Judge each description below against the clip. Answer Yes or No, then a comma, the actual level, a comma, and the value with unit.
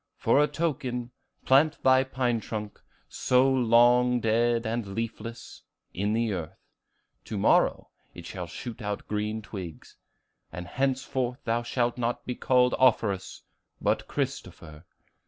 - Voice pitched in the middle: No, low, 120 Hz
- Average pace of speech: No, slow, 130 wpm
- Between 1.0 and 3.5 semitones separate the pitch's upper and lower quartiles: Yes, average, 2.9 semitones